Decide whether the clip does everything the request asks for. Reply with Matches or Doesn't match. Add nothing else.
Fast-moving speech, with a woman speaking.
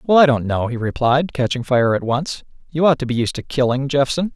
Doesn't match